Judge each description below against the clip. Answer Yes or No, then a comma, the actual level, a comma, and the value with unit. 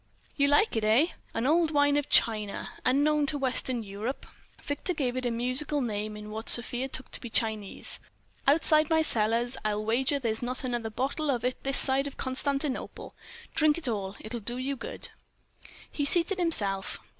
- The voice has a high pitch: Yes, very high, 255 Hz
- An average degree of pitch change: Yes, average, 4.4 semitones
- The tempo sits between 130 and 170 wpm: No, average, 180 wpm